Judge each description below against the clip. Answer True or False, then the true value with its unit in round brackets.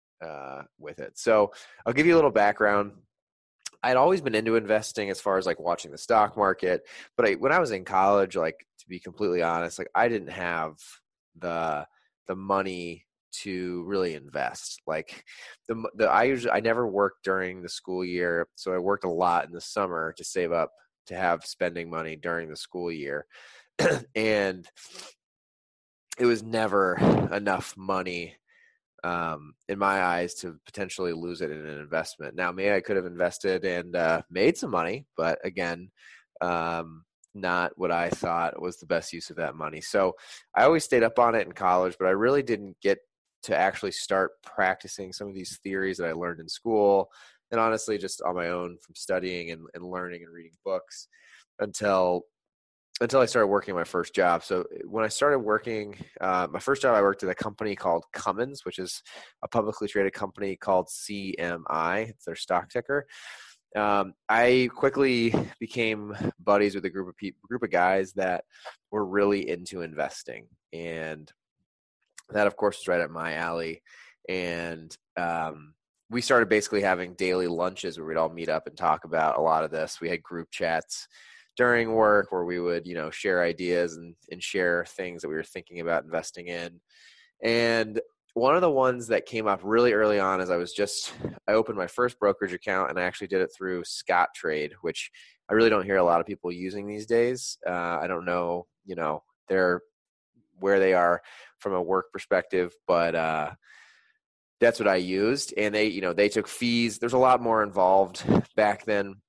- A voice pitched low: True (95 Hz)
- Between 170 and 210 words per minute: True (185 wpm)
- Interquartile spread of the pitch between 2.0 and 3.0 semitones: False (3.5 semitones)